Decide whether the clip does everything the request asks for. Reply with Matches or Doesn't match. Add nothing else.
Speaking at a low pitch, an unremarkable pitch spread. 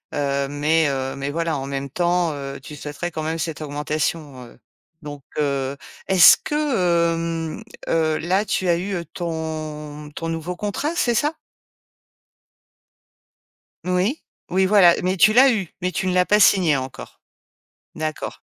Doesn't match